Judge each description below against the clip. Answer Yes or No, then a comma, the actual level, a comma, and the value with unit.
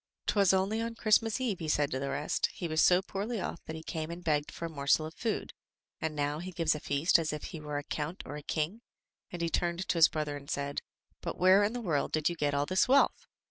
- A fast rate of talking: Yes, fast, 260 wpm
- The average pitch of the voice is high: No, medium, 165 Hz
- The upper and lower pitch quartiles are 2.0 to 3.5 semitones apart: No, average, 4.2 semitones